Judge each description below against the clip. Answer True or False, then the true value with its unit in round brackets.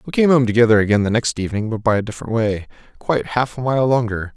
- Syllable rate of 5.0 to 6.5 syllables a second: False (6.9 syllables/s)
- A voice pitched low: True (115 Hz)